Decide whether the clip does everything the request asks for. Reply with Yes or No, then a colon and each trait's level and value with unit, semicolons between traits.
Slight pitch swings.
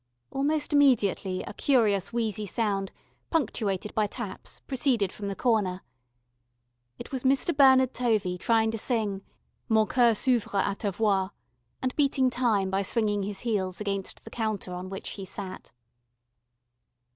No: average, 4.2 semitones